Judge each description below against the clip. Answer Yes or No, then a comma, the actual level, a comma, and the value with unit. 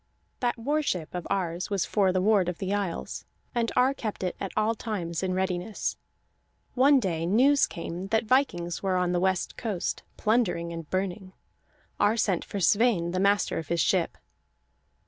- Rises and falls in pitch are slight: No, average, 4.0 semitones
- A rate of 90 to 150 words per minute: No, average, 175 wpm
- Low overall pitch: No, high, 190 Hz